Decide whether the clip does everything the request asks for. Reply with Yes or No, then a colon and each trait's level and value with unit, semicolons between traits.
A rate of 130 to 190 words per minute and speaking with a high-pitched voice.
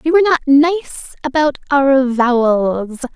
Yes: slow, 135 wpm; very high, 275 Hz